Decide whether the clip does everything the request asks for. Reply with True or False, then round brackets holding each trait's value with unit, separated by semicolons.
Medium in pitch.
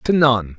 False (120 Hz)